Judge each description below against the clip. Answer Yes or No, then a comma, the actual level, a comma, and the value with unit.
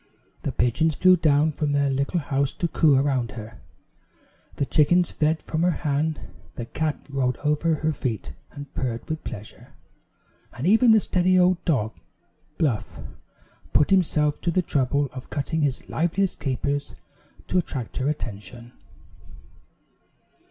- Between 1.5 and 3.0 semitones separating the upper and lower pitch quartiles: No, average, 3.6 semitones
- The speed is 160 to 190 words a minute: No, average, 145 wpm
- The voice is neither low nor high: Yes, medium, 145 Hz